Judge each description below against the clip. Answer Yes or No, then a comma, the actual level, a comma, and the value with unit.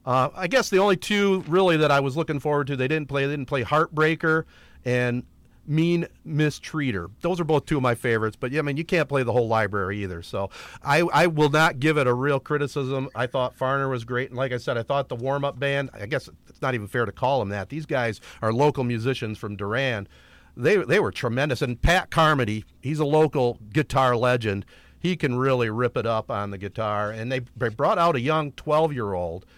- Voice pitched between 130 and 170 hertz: Yes, low, 135 Hz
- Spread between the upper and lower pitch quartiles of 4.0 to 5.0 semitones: Yes, average, 4.5 semitones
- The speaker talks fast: Yes, fast, 215 wpm